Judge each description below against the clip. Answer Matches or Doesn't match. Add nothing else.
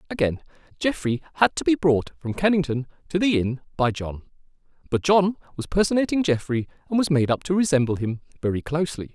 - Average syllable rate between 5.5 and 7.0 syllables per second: Matches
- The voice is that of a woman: Doesn't match